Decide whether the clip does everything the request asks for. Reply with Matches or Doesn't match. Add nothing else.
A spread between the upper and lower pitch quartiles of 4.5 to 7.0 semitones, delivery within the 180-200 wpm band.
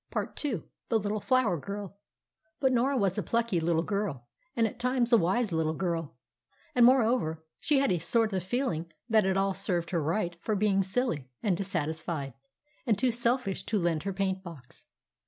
Matches